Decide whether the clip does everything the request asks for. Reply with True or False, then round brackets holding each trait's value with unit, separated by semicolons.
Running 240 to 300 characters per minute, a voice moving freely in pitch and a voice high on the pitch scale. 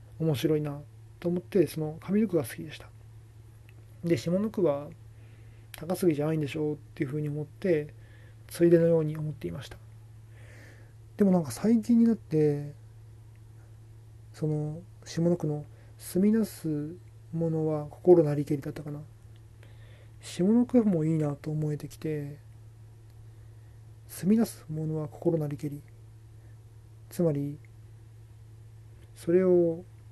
False (250 characters per minute; 6.2 semitones; 140 Hz)